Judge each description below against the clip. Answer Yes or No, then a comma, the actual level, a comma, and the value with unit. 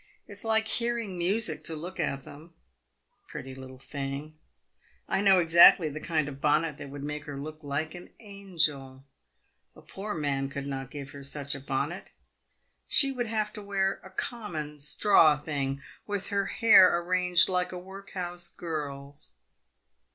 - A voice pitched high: No, medium, 160 Hz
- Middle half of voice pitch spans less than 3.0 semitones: No, average, 5.3 semitones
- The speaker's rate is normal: Yes, average, 160 wpm